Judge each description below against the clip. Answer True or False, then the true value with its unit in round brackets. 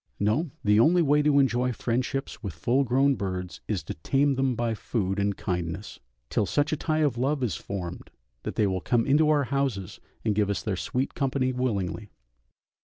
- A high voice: False (120 Hz)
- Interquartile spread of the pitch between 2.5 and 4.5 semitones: False (5.5 semitones)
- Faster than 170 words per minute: True (190 wpm)